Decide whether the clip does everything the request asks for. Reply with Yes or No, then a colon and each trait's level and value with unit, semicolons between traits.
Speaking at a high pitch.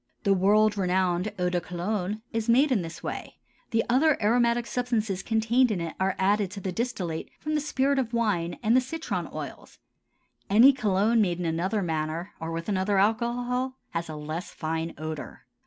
Yes: high, 205 Hz